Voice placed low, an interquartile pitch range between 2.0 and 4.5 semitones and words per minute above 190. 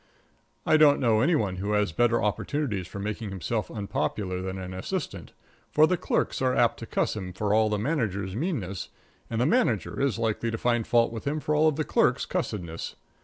No: low, 110 Hz; average, 5.2 semitones; average, 200 wpm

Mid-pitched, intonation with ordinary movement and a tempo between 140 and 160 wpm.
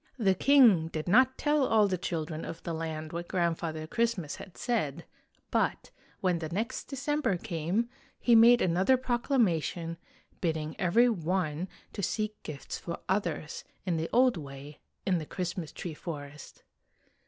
No: medium, 180 Hz; wide, 6.1 semitones; average, 155 wpm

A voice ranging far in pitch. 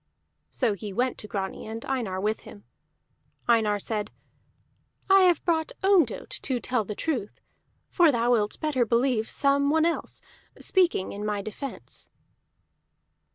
Yes: wide, 5.7 semitones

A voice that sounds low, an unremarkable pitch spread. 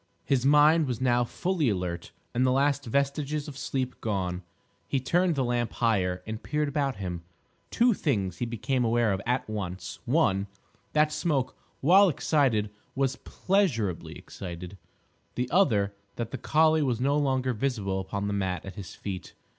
No: low, 125 Hz; wide, 6.1 semitones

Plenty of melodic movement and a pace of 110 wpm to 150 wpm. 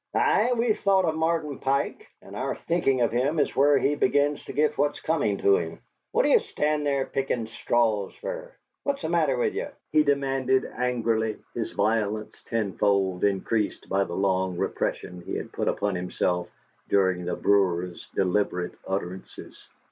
No: wide, 7.0 semitones; average, 165 wpm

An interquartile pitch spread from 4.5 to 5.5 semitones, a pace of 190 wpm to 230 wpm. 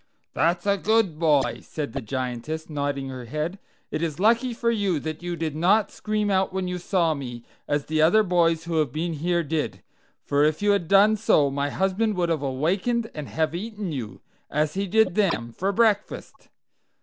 Yes: average, 5.2 semitones; average, 195 wpm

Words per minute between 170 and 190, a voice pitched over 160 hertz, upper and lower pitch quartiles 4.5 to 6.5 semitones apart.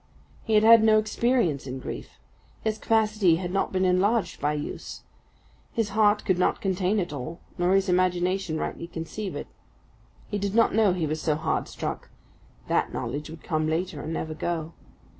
Yes: average, 180 wpm; medium, 185 Hz; average, 4.8 semitones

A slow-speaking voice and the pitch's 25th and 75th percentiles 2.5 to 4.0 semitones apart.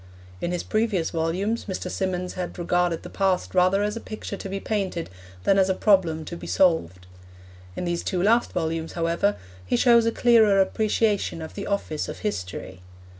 No: average, 180 wpm; average, 3.5 semitones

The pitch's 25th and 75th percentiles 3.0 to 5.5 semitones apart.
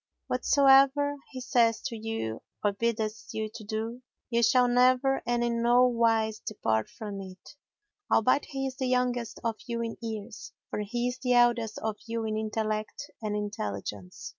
No: narrow, 2.5 semitones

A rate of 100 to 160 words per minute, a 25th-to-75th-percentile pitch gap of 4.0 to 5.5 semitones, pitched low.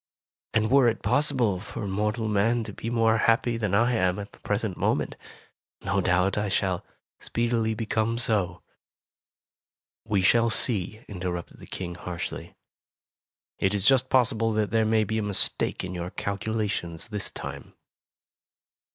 No: average, 150 wpm; average, 3.0 semitones; low, 110 Hz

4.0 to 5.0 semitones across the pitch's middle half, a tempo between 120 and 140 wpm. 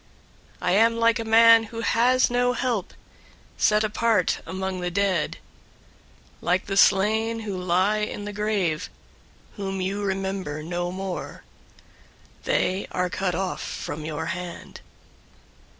No: average, 3.4 semitones; slow, 135 wpm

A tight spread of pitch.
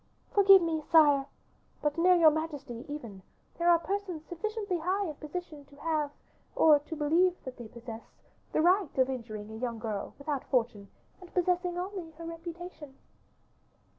No: average, 4.7 semitones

